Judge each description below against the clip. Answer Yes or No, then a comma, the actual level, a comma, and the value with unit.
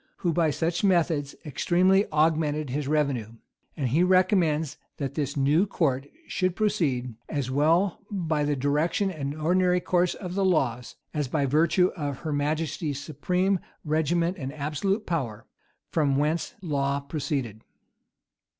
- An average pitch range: Yes, average, 3.8 semitones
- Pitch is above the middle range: No, medium, 155 Hz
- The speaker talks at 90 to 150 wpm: Yes, average, 140 wpm